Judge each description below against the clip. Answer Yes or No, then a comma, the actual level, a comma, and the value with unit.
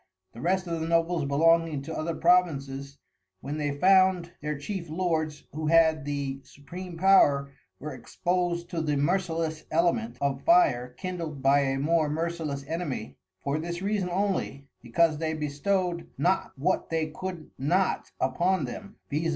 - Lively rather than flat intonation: No, average, 3.8 semitones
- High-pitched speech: No, medium, 160 Hz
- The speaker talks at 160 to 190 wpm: No, average, 150 wpm